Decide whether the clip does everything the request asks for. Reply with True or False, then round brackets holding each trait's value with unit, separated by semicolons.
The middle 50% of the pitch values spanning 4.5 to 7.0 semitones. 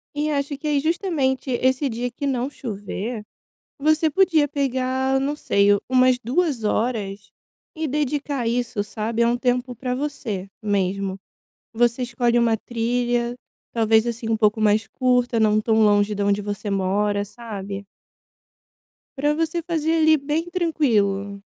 True (4.9 semitones)